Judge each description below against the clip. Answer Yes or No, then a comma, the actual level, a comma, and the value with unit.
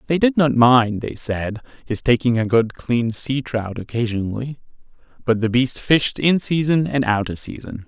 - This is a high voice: No, low, 125 Hz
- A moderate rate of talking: Yes, average, 185 wpm